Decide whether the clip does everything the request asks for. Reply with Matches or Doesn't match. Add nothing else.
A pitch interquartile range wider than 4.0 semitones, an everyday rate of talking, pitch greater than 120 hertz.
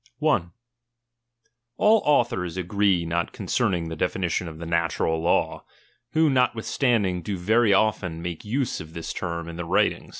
Doesn't match